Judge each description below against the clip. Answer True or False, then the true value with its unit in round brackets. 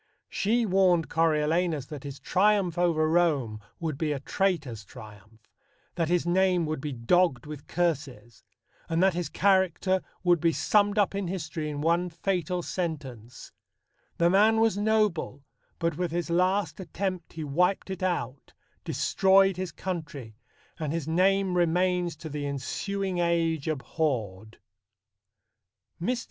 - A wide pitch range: False (3.8 semitones)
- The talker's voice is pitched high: False (170 Hz)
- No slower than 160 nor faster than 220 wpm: False (140 wpm)